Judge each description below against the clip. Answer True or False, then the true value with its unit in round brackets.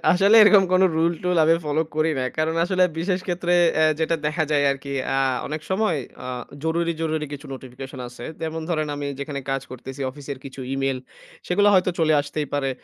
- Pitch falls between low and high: True (155 Hz)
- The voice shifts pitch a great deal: False (3.8 semitones)